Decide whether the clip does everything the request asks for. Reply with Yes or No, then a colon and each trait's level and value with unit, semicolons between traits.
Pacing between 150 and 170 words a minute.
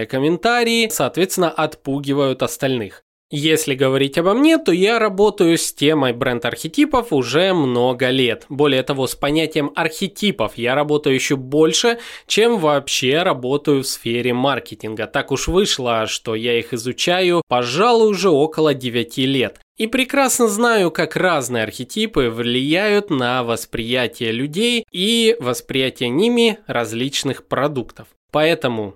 No: average, 125 wpm